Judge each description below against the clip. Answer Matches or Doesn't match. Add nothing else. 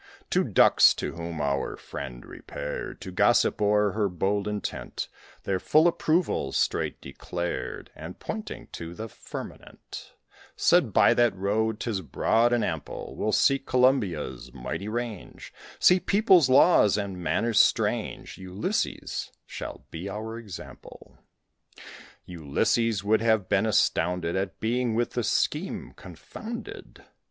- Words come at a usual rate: Doesn't match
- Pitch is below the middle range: Matches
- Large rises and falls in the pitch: Doesn't match